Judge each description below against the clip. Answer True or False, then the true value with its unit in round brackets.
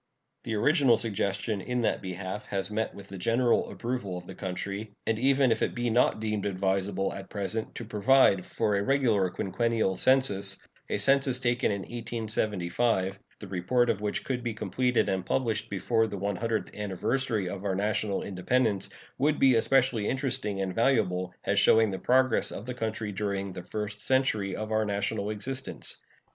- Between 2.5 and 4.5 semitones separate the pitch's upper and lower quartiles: True (3.6 semitones)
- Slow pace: False (175 wpm)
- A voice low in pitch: True (110 Hz)